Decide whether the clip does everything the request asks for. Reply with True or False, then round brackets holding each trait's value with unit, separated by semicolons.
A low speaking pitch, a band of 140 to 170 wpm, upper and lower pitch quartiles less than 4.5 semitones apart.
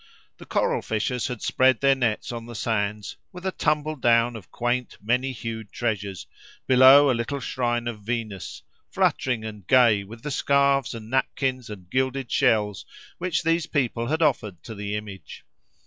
True (120 Hz; 165 wpm; 3.6 semitones)